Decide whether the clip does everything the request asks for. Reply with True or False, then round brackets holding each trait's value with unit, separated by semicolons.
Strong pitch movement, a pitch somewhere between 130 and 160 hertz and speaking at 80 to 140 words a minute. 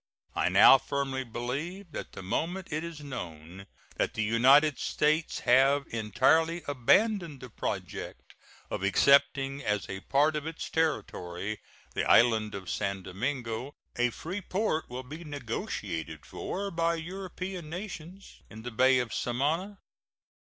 True (6.4 semitones; 140 Hz; 135 wpm)